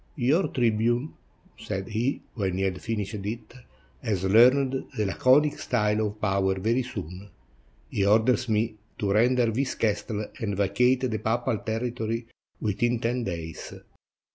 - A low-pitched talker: Yes, low, 110 Hz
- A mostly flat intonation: No, average, 3.2 semitones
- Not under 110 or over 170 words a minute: Yes, average, 140 wpm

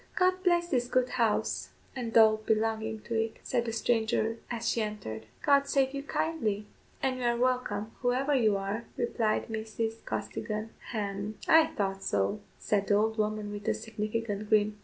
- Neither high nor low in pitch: No, high, 225 Hz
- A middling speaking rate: Yes, average, 170 wpm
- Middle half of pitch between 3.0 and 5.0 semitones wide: No, narrow, 2.6 semitones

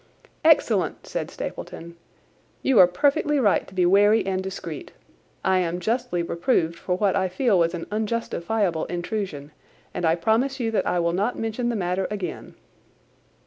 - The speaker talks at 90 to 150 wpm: No, average, 160 wpm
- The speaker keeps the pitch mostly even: No, average, 4.3 semitones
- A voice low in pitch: No, high, 190 Hz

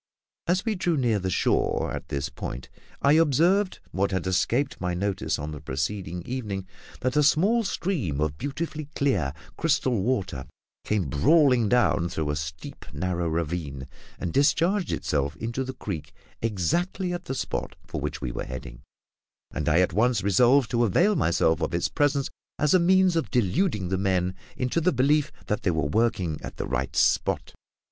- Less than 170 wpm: No, average, 175 wpm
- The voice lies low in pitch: Yes, low, 105 Hz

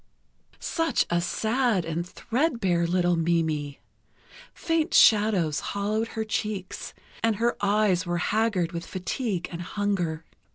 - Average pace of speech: No, slow, 125 wpm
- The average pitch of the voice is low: No, high, 190 Hz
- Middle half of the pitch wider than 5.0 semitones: No, average, 4.3 semitones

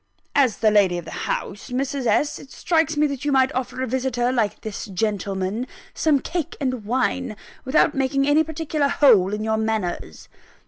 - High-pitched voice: Yes, very high, 255 Hz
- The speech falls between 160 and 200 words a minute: Yes, average, 180 wpm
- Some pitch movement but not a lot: Yes, average, 4.6 semitones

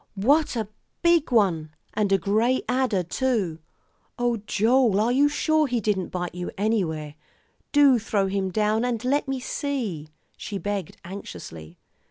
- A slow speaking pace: No, average, 150 wpm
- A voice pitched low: No, high, 215 Hz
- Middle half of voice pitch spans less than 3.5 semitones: No, average, 5.2 semitones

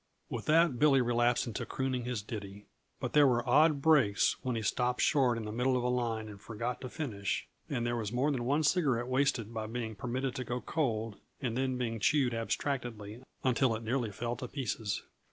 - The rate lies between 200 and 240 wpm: Yes, fast, 205 wpm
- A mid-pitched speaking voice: No, low, 120 Hz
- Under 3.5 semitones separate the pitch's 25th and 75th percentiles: Yes, average, 2.8 semitones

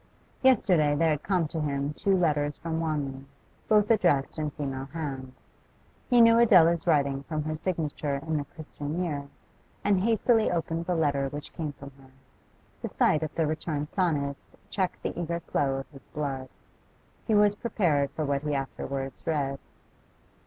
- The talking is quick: No, average, 165 wpm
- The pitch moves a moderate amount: Yes, average, 3.5 semitones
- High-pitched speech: No, medium, 155 Hz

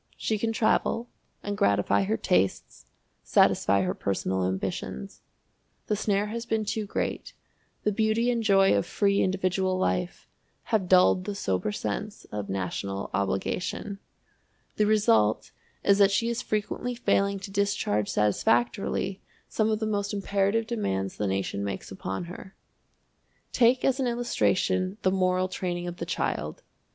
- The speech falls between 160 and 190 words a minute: No, average, 145 wpm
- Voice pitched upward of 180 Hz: Yes, high, 190 Hz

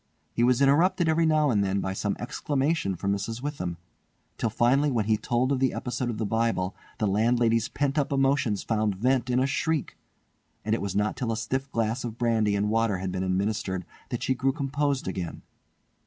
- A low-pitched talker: Yes, low, 115 Hz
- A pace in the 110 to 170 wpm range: No, average, 200 wpm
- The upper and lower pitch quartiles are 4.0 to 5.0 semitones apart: Yes, average, 4.6 semitones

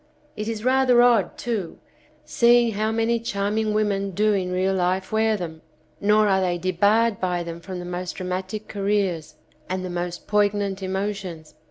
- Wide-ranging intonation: No, average, 2.9 semitones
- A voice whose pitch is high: Yes, high, 200 Hz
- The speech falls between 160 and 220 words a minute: Yes, average, 170 wpm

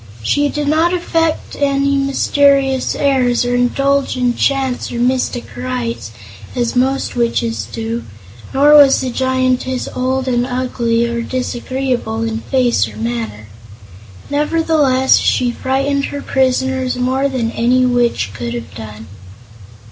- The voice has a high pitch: Yes, very high, 255 Hz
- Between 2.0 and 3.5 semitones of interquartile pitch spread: Yes, average, 2.7 semitones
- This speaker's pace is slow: Yes, slow, 130 wpm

